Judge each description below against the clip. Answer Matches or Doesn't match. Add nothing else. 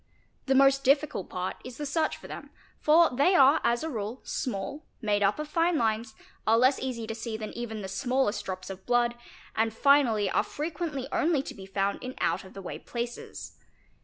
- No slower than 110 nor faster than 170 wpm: Doesn't match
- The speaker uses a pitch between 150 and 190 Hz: Doesn't match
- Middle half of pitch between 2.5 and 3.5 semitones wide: Doesn't match